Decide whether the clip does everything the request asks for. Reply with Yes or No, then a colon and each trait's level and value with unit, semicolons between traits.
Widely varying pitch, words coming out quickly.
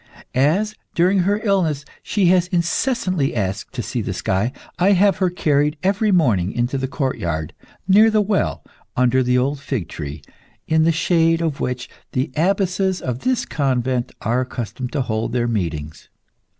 No: wide, 7.2 semitones; average, 165 wpm